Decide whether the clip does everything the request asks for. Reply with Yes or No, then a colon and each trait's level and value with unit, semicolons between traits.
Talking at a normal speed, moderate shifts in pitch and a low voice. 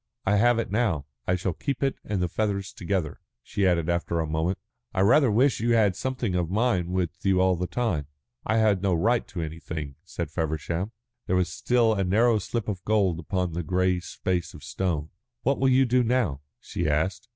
No: fast, 210 wpm; average, 4.6 semitones; very low, 95 Hz